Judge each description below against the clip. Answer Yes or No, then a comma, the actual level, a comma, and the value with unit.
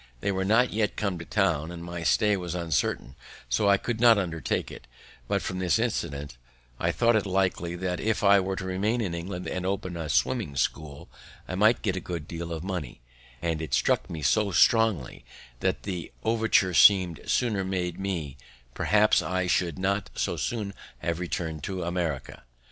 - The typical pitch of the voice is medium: No, very low, 90 Hz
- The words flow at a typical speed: Yes, average, 190 wpm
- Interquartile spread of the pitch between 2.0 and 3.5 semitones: Yes, average, 3.1 semitones